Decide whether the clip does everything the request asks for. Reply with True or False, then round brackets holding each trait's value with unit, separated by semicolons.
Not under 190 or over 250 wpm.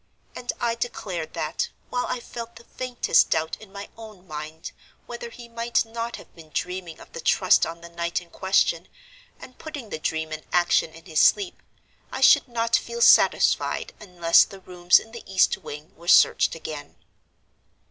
False (180 wpm)